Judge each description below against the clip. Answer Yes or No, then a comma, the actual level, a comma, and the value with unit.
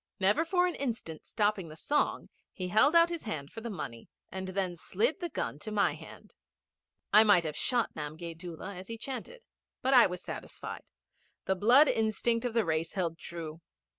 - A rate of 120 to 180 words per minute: No, average, 190 wpm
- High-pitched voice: Yes, high, 205 Hz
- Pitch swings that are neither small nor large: No, wide, 5.9 semitones